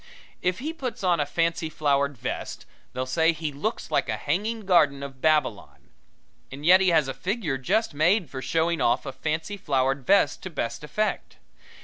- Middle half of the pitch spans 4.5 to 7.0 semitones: Yes, average, 5.1 semitones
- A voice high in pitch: No, medium, 160 Hz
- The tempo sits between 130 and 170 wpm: No, average, 185 wpm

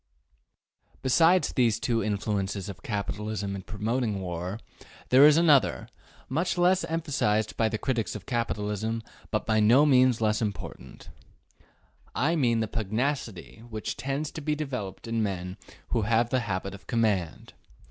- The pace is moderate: Yes, average, 145 wpm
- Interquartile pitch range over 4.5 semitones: No, average, 4.2 semitones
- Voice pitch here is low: Yes, low, 115 Hz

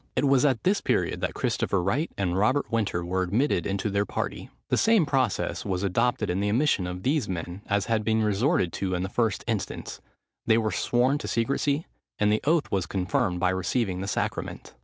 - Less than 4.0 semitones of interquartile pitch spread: No, wide, 5.5 semitones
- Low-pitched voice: Yes, low, 105 Hz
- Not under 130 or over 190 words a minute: No, average, 200 wpm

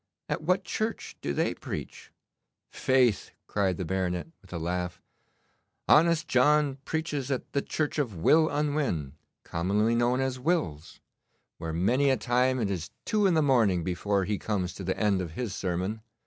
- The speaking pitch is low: Yes, low, 115 Hz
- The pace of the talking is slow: No, average, 165 wpm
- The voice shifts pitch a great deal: Yes, wide, 7.7 semitones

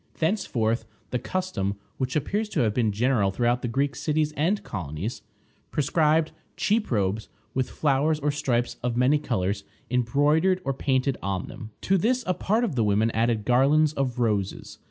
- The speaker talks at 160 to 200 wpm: Yes, average, 165 wpm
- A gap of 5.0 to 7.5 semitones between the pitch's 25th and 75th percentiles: Yes, wide, 5.4 semitones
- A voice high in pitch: No, low, 130 Hz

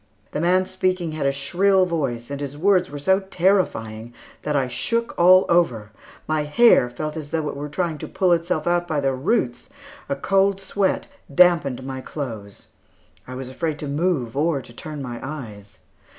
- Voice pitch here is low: No, medium, 150 Hz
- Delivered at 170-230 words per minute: Yes, average, 180 wpm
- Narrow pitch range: No, average, 5.3 semitones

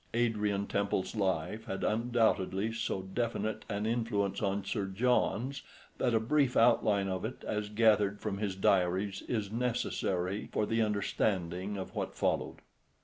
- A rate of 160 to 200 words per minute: No, average, 145 wpm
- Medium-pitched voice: No, low, 105 Hz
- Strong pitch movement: No, narrow, 2.6 semitones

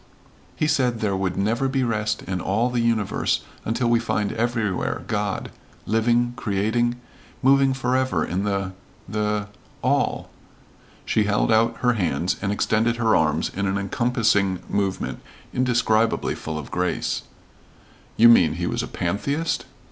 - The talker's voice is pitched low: Yes, low, 110 Hz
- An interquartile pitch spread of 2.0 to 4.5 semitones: Yes, average, 3.5 semitones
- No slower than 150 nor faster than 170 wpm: No, average, 140 wpm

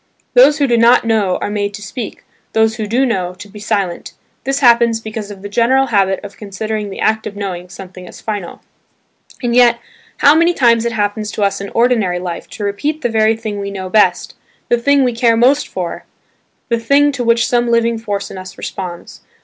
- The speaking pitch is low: No, high, 220 Hz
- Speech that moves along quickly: Yes, fast, 210 wpm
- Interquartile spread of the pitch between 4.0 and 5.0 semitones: No, average, 3.1 semitones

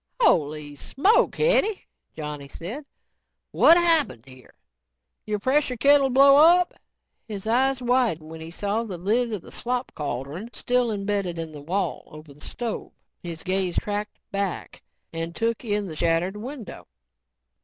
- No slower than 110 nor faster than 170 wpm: Yes, average, 145 wpm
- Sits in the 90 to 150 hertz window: No, high, 205 Hz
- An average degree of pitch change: No, wide, 7.3 semitones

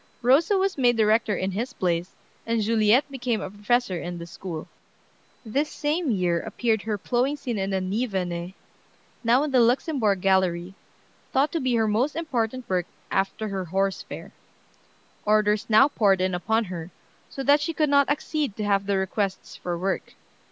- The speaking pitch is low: No, high, 215 Hz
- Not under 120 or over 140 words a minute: No, average, 175 wpm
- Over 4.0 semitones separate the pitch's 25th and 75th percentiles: Yes, average, 5.2 semitones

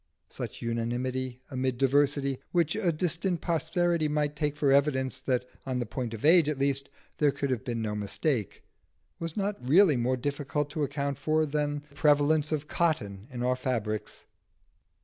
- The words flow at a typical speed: Yes, average, 170 wpm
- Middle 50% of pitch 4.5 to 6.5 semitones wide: No, average, 3.3 semitones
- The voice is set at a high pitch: No, medium, 140 Hz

